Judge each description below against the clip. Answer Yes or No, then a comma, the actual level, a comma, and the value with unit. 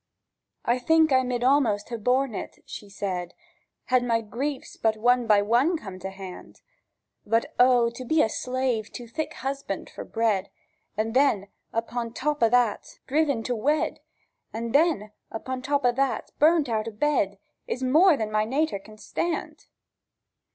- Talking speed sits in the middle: Yes, average, 160 wpm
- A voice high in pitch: Yes, high, 245 Hz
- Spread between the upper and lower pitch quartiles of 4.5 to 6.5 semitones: No, average, 4.1 semitones